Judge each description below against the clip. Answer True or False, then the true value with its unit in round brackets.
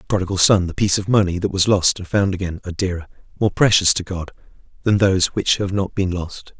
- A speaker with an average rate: False (235 wpm)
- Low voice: True (95 Hz)